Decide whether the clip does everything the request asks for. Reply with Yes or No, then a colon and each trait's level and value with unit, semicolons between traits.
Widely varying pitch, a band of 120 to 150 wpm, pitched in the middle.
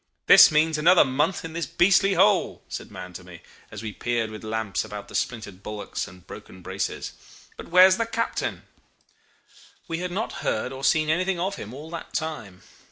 No: wide, 8.8 semitones; average, 185 wpm; medium, 150 Hz